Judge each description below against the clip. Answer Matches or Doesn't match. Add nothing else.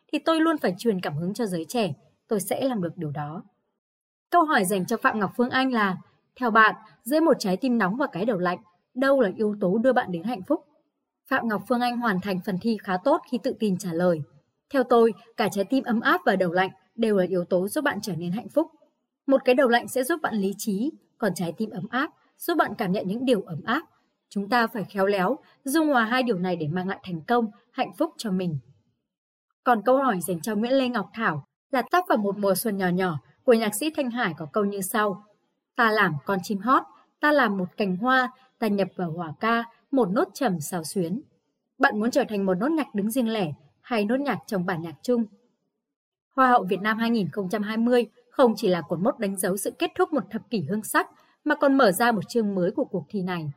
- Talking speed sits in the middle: Matches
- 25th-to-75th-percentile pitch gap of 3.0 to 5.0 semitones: Doesn't match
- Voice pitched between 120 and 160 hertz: Doesn't match